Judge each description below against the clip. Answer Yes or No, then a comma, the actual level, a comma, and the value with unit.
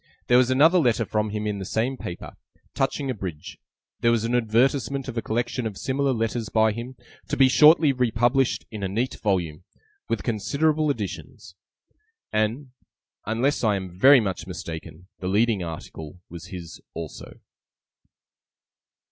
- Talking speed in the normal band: Yes, average, 155 wpm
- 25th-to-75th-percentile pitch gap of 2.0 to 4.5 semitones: No, average, 5.3 semitones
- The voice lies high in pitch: No, low, 115 Hz